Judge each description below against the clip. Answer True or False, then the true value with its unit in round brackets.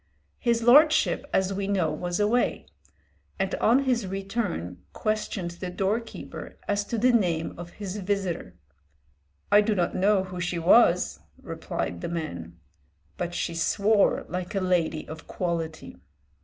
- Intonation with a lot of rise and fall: False (3.7 semitones)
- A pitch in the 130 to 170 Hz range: False (190 Hz)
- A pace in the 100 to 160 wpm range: True (140 wpm)